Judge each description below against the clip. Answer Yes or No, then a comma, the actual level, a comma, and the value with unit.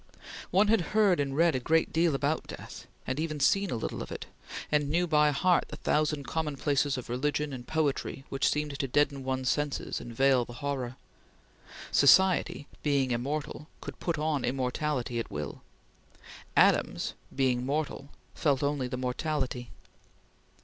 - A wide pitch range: No, average, 2.9 semitones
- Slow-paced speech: No, average, 155 wpm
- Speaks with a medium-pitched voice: Yes, medium, 145 Hz